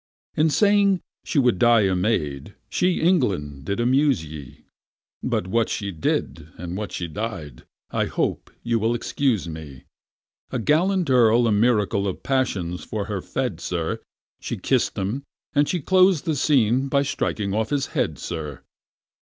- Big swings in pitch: Yes, wide, 7.6 semitones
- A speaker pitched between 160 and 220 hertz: No, low, 110 Hz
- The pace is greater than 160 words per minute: No, average, 155 wpm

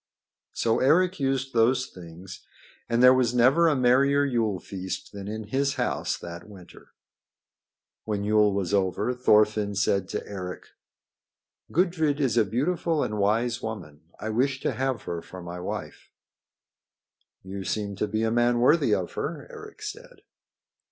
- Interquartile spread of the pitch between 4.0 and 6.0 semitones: Yes, average, 5.0 semitones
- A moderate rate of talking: Yes, average, 150 wpm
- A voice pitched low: Yes, low, 115 Hz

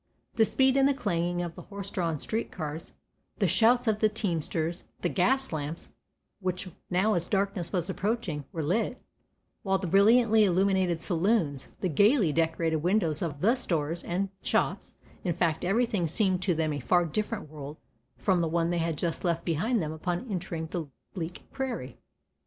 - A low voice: No, medium, 180 Hz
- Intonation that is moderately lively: Yes, average, 4.2 semitones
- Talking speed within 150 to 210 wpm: Yes, average, 170 wpm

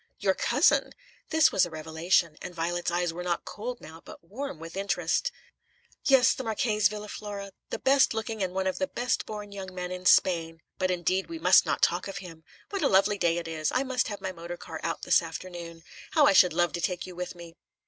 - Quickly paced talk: Yes, fast, 225 wpm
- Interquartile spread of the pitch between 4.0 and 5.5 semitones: No, average, 3.6 semitones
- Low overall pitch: No, medium, 185 Hz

